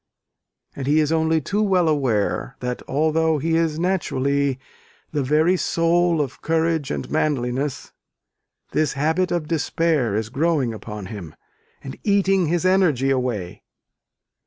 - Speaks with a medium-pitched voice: Yes, medium, 155 Hz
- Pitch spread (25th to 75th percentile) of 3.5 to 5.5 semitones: Yes, average, 4.0 semitones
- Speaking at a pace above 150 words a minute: No, slow, 135 wpm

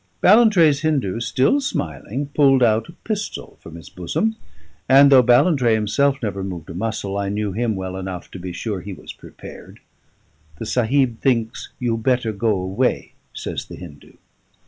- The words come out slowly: No, average, 165 wpm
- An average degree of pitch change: No, wide, 6.0 semitones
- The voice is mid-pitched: No, low, 115 Hz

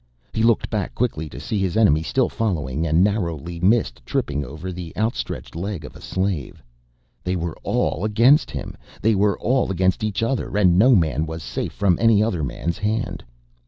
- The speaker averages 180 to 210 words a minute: Yes, average, 185 wpm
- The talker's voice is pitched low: Yes, very low, 95 Hz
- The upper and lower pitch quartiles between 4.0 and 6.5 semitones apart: Yes, average, 5.0 semitones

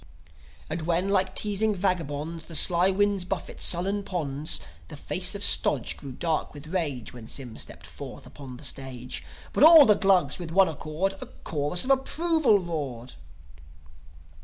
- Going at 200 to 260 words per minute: No, average, 160 wpm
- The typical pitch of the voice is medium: Yes, medium, 170 Hz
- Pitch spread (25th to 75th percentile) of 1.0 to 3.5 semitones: No, average, 5.1 semitones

